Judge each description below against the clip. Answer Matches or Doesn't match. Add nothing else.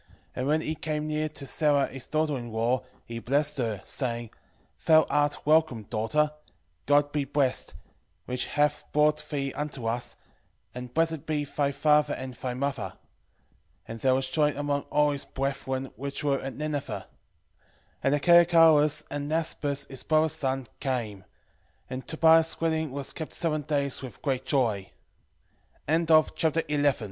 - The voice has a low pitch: Doesn't match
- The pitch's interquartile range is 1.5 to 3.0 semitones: Matches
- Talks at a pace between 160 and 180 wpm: Doesn't match